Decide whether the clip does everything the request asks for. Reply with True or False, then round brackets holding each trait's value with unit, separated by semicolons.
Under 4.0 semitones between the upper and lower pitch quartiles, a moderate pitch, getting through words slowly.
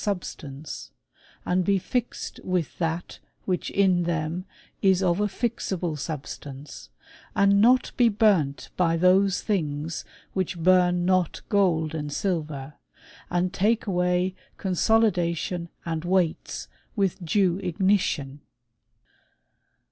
True (3.2 semitones; 180 Hz; 115 wpm)